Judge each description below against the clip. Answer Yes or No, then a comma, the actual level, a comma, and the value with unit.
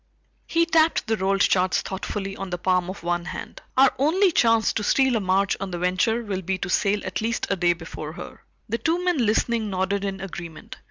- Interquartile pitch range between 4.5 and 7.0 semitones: No, average, 3.9 semitones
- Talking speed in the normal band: No, fast, 215 wpm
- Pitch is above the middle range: Yes, high, 195 Hz